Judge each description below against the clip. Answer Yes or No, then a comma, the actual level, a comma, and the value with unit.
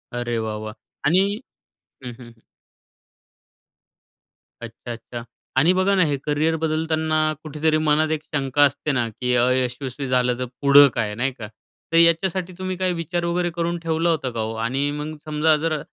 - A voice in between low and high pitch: Yes, medium, 150 Hz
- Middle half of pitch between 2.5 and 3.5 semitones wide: No, average, 4.7 semitones